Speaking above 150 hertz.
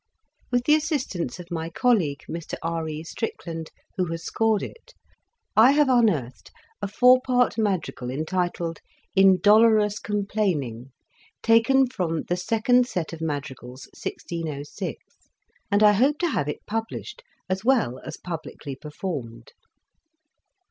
Yes: medium, 185 Hz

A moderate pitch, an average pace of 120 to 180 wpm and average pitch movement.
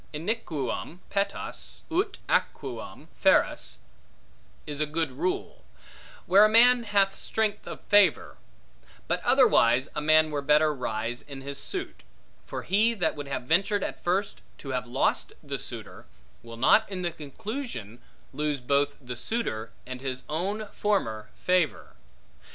No: medium, 155 Hz; average, 140 wpm; wide, 7.3 semitones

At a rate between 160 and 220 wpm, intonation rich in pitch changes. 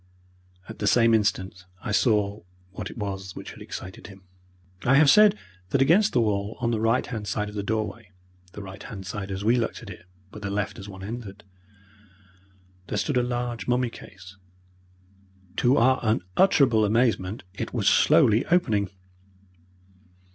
No: average, 170 wpm; average, 3.5 semitones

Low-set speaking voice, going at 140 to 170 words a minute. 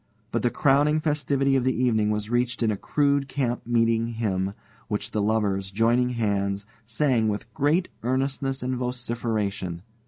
Yes: low, 120 Hz; average, 155 wpm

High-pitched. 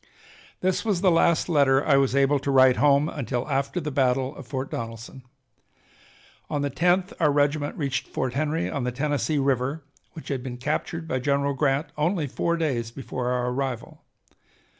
No: medium, 140 Hz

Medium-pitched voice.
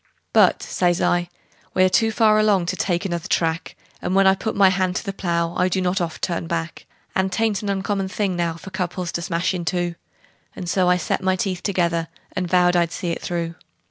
Yes: medium, 180 Hz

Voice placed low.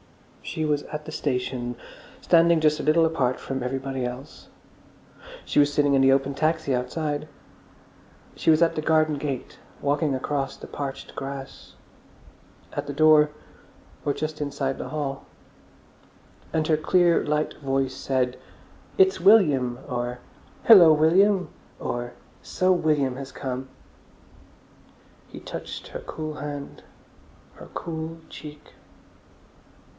No: medium, 145 Hz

